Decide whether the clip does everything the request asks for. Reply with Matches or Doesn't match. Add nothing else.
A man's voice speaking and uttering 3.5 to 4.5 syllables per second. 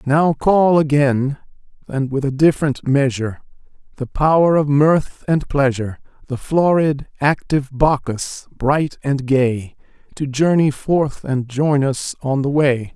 Matches